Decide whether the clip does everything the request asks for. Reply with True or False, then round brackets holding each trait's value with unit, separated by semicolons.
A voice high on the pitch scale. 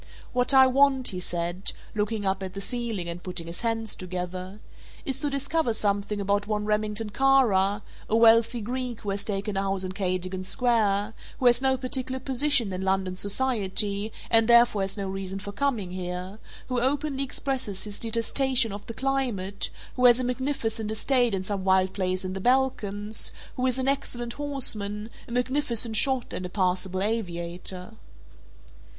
True (215 Hz)